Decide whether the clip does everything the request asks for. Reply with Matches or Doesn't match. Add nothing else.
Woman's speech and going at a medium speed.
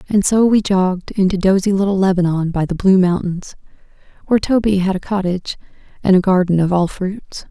Matches